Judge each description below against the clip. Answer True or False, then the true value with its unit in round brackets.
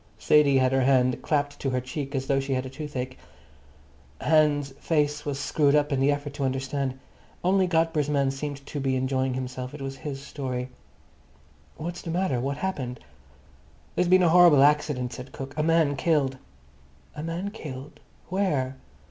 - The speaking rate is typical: True (170 wpm)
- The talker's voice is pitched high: False (140 Hz)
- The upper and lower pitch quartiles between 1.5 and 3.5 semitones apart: True (2.4 semitones)